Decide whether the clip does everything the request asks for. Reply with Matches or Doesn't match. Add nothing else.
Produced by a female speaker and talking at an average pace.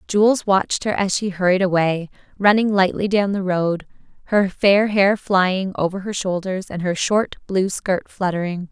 Matches